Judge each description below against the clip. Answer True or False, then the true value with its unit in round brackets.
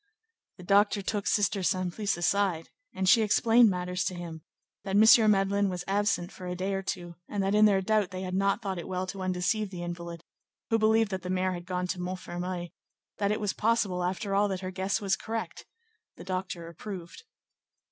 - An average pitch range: False (2.3 semitones)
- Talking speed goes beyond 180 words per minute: True (200 wpm)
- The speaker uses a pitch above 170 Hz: True (190 Hz)